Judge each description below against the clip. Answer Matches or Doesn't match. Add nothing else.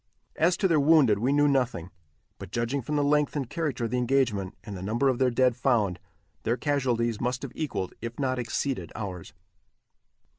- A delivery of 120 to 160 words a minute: Doesn't match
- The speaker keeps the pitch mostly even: Doesn't match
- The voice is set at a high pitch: Doesn't match